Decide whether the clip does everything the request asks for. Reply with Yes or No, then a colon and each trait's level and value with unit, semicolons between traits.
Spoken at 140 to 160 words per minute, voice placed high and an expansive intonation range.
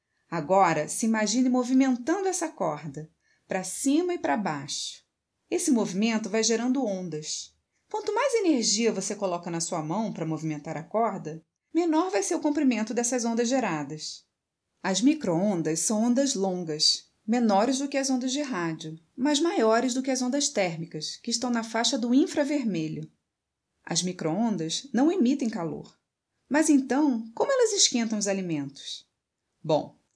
Yes: average, 145 wpm; high, 225 Hz; wide, 7.8 semitones